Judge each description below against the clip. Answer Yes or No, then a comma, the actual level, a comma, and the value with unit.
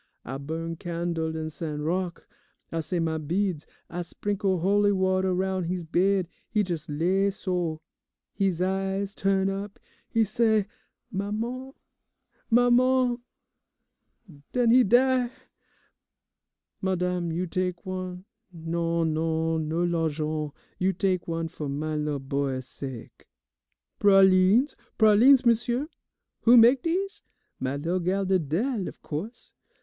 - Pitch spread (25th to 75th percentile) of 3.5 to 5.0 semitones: Yes, average, 4.0 semitones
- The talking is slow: Yes, slow, 120 wpm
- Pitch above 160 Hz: Yes, medium, 185 Hz